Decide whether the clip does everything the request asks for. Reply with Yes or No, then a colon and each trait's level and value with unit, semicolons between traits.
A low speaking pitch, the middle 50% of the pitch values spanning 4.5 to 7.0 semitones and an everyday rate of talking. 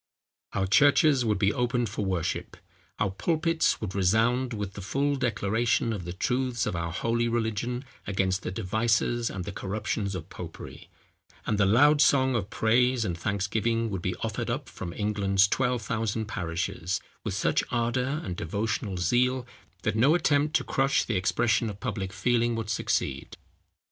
No: low, 110 Hz; average, 3.9 semitones; average, 165 wpm